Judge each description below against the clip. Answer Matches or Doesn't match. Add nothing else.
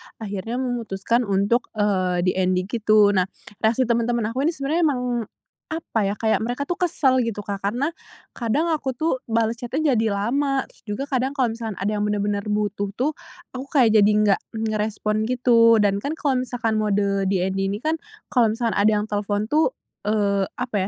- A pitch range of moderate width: Matches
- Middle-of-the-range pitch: Doesn't match